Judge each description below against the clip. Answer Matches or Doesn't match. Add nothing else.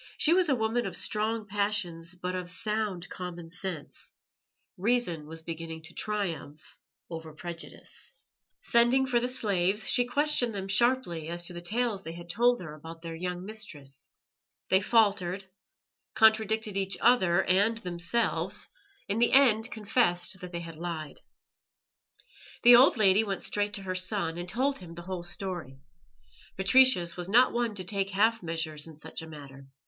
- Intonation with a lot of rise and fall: Doesn't match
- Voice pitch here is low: Doesn't match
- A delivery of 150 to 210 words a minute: Matches